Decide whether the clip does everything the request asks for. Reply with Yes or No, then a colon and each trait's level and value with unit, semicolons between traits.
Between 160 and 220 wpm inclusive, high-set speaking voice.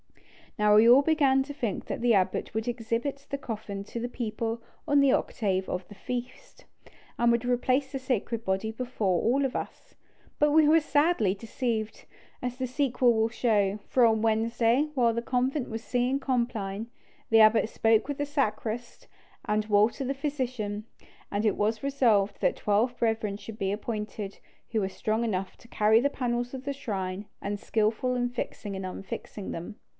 Yes: average, 180 wpm; high, 230 Hz